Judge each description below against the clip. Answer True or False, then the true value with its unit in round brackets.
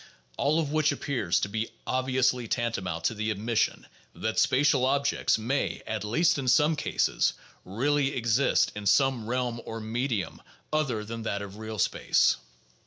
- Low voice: True (120 Hz)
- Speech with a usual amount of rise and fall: True (4.1 semitones)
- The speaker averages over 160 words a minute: False (155 wpm)